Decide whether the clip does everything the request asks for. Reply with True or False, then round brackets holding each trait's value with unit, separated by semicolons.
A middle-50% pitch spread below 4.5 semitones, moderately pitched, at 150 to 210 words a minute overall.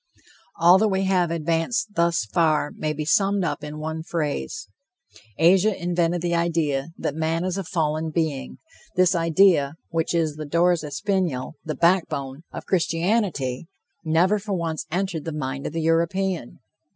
True (2.9 semitones; 165 Hz; 155 wpm)